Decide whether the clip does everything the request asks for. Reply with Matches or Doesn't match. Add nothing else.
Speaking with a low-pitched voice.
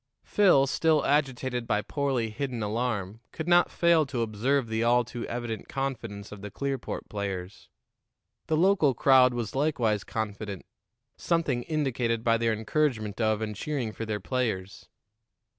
Matches